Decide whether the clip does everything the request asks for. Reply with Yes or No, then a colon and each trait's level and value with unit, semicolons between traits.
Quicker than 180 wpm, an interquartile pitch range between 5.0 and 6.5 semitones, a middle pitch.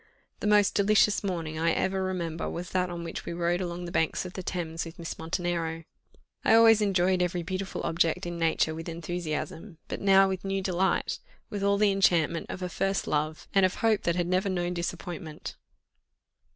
No: average, 190 wpm; narrow, 2.5 semitones; medium, 180 Hz